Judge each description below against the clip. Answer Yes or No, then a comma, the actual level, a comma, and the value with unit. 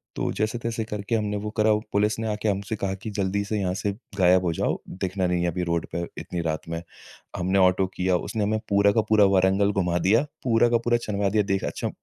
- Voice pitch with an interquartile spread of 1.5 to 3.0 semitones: Yes, average, 2.7 semitones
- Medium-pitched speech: No, low, 100 Hz